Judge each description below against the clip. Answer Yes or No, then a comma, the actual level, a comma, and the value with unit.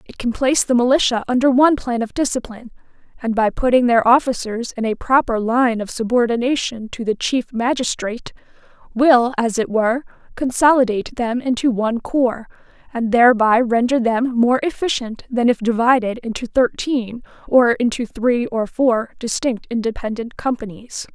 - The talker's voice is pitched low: No, high, 240 Hz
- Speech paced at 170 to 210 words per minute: No, average, 150 wpm